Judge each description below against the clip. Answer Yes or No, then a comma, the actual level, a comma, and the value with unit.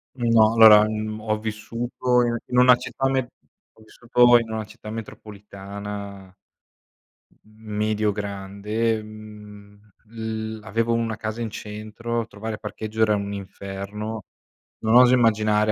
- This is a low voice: Yes, low, 110 Hz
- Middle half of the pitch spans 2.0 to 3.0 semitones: No, narrow, 1.5 semitones